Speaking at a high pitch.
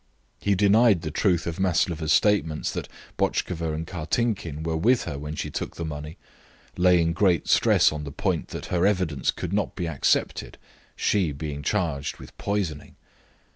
No: very low, 85 Hz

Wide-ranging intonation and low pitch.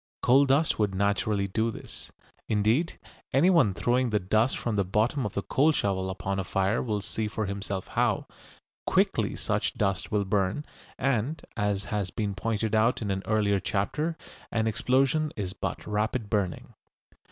No: average, 3.6 semitones; low, 105 Hz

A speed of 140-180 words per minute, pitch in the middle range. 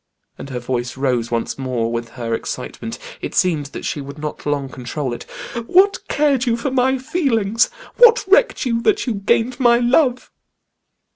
No: average, 170 wpm; high, 200 Hz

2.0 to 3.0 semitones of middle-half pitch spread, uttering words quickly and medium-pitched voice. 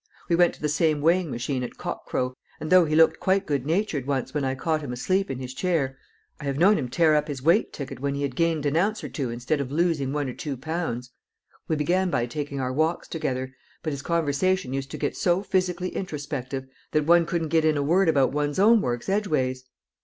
No: average, 4.2 semitones; fast, 235 wpm; medium, 150 Hz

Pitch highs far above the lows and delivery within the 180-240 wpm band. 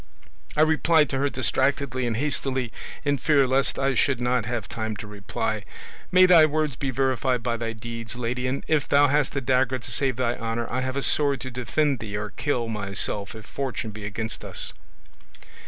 No: average, 3.4 semitones; average, 195 wpm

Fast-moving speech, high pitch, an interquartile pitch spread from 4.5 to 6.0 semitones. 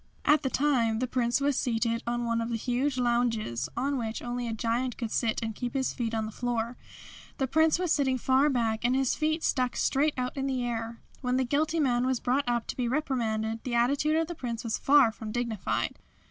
No: fast, 225 wpm; high, 245 Hz; average, 2.7 semitones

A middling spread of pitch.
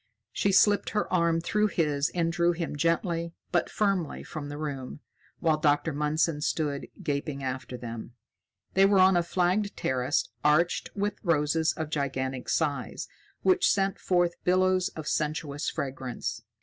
Yes: average, 3.8 semitones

